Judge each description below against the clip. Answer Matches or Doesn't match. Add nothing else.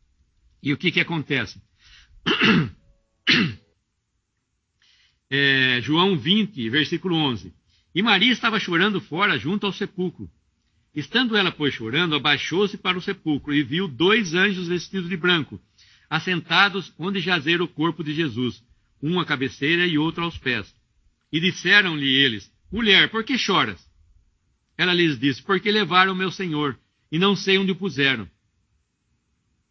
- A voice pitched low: Doesn't match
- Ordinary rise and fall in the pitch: Doesn't match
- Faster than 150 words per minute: Doesn't match